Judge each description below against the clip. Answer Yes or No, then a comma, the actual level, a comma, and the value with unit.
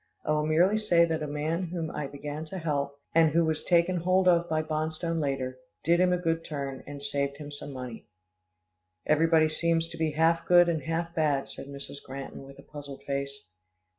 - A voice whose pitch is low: No, medium, 155 Hz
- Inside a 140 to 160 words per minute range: No, average, 200 wpm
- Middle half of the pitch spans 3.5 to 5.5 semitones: No, average, 2.9 semitones